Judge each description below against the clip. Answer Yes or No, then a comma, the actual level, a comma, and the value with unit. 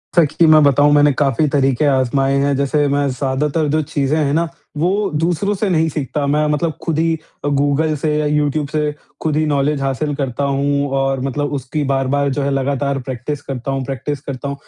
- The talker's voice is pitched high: No, medium, 145 Hz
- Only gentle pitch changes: Yes, narrow, 1.8 semitones